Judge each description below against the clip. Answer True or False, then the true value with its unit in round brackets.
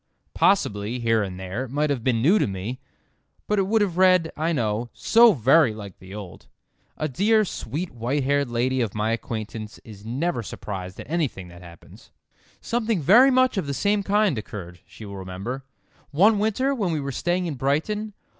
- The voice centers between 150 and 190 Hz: False (135 Hz)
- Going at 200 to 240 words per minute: False (190 wpm)